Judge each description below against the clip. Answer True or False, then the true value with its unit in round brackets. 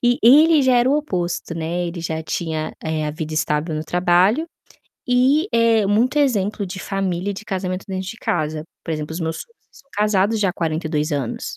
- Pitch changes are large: True (6.0 semitones)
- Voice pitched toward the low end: False (185 Hz)